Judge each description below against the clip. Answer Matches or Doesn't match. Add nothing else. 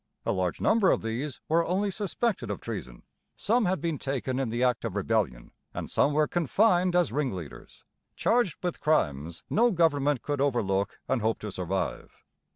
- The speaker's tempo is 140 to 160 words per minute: Doesn't match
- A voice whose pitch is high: Doesn't match